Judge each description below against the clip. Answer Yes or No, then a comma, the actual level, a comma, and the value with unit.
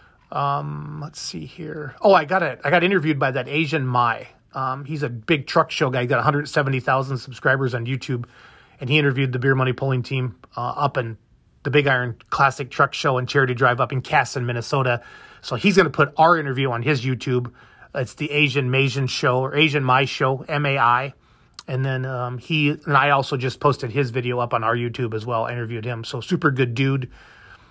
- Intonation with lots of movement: No, average, 2.7 semitones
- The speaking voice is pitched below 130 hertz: No, low, 135 Hz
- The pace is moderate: No, fast, 210 wpm